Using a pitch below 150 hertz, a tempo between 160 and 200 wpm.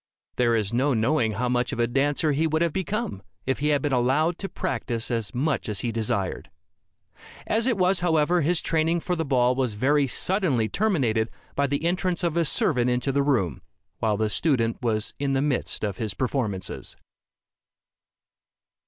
Yes: low, 135 Hz; average, 180 wpm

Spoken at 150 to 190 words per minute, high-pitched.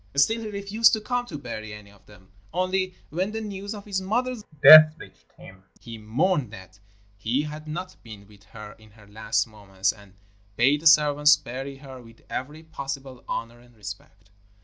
No: average, 185 wpm; low, 135 Hz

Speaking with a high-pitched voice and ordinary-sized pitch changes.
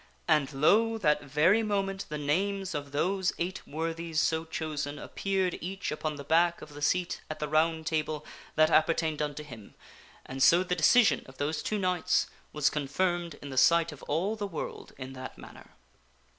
No: medium, 160 Hz; average, 3.6 semitones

